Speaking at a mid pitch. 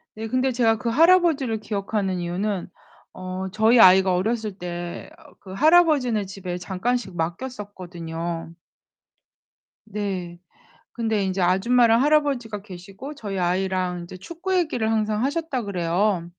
No: high, 205 Hz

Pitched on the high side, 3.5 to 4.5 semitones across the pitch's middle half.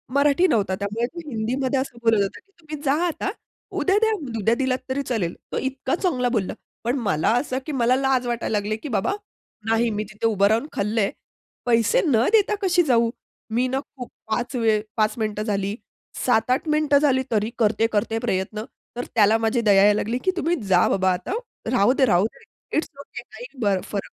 Yes: high, 235 Hz; average, 4.2 semitones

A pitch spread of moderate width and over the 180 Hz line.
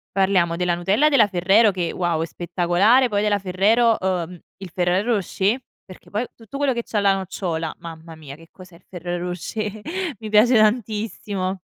Yes: average, 3.5 semitones; high, 190 Hz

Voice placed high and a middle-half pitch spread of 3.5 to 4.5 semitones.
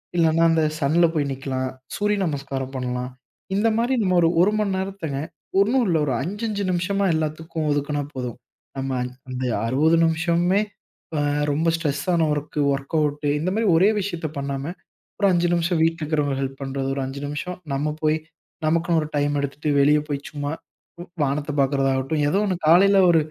No: medium, 155 Hz; average, 3.9 semitones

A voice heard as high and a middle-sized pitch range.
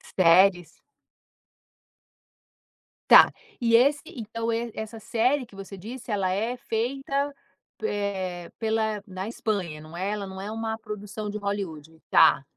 Yes: high, 210 Hz; average, 3.3 semitones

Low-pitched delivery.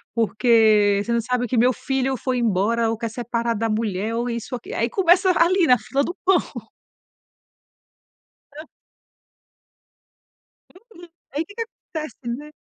No: high, 240 Hz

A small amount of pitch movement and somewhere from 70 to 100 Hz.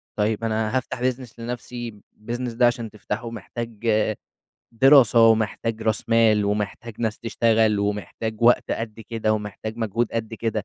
No: narrow, 1.6 semitones; low, 115 Hz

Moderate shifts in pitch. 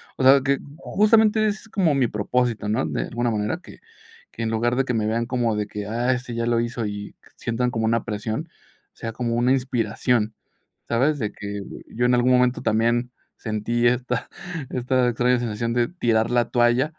No: narrow, 2.1 semitones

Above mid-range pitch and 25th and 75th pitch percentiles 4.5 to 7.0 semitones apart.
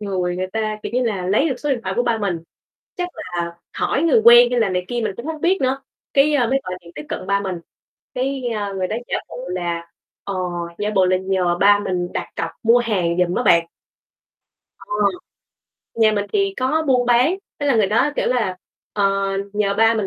Yes: high, 210 Hz; average, 5.1 semitones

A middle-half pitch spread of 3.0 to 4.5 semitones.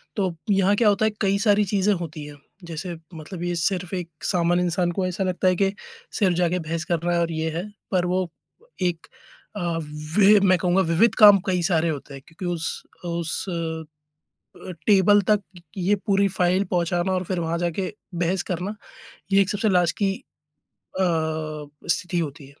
No: narrow, 2.5 semitones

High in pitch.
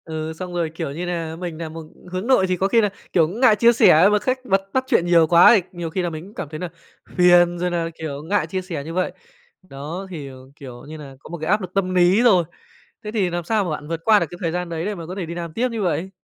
No: medium, 175 Hz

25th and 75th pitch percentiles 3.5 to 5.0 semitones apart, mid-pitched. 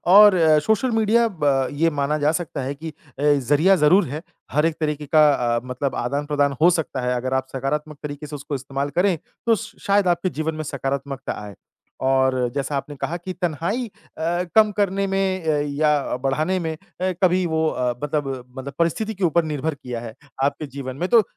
Yes: average, 4.2 semitones; medium, 150 Hz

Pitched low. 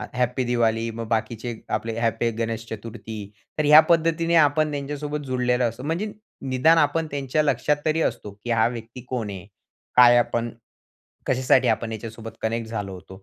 Yes: low, 120 Hz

